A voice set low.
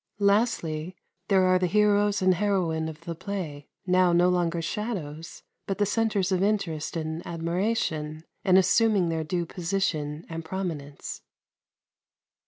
No: medium, 180 Hz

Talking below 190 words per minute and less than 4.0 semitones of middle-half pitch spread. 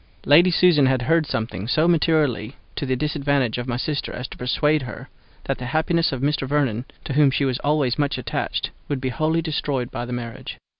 No: fast, 205 wpm; average, 3.5 semitones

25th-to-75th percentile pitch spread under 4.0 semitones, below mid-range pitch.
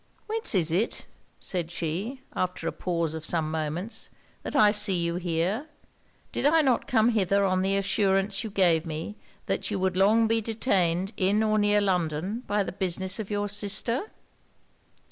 No: average, 3.5 semitones; high, 195 Hz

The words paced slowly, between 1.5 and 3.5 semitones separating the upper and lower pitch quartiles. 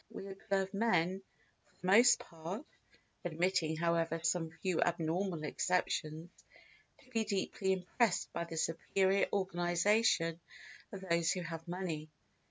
Yes: slow, 125 wpm; average, 2.8 semitones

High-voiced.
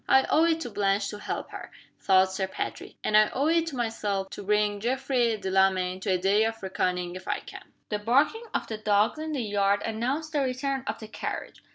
Yes: high, 215 Hz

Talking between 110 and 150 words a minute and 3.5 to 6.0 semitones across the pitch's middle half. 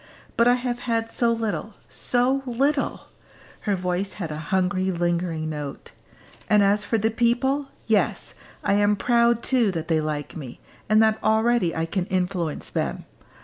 No: average, 160 wpm; average, 5.2 semitones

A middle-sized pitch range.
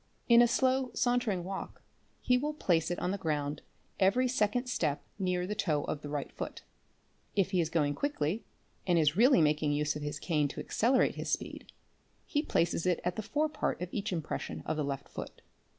No: wide, 8.0 semitones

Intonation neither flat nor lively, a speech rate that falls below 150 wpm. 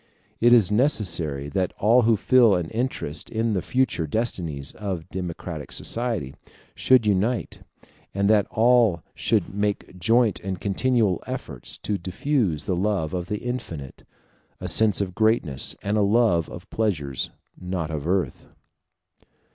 Yes: average, 4.8 semitones; average, 140 wpm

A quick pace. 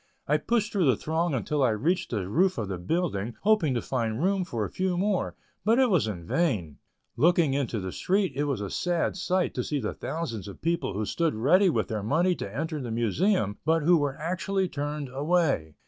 Yes: fast, 220 wpm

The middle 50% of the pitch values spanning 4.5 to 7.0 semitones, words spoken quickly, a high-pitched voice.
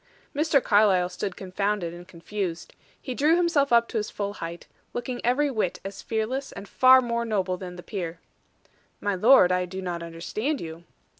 No: wide, 5.4 semitones; average, 175 wpm; high, 205 Hz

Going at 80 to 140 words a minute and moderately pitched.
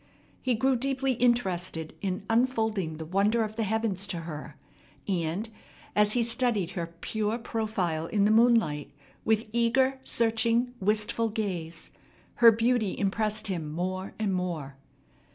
No: slow, 135 wpm; high, 215 Hz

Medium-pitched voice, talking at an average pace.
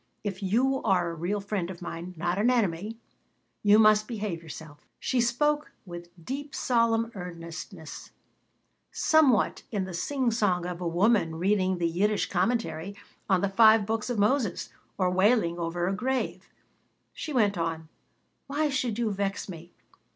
No: high, 200 Hz; average, 150 wpm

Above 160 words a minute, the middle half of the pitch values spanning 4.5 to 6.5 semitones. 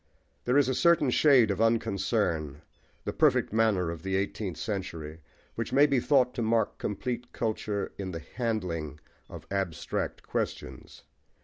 No: average, 145 wpm; average, 5.2 semitones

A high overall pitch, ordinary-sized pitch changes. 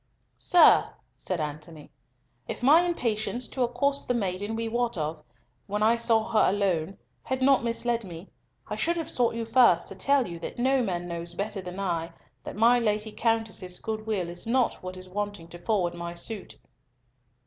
Yes: high, 215 Hz; average, 5.0 semitones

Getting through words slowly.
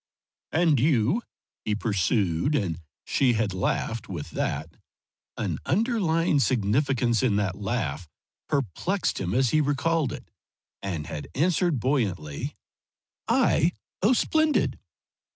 Yes: slow, 115 wpm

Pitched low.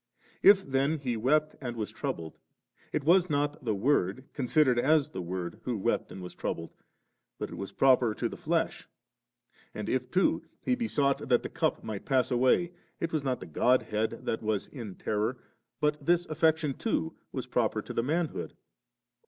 Yes: low, 130 Hz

